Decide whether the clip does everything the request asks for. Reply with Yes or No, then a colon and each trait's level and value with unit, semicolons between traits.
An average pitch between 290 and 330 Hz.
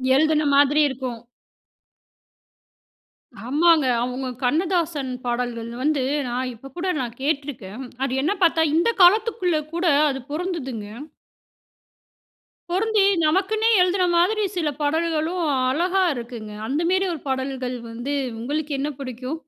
Yes: very high, 295 Hz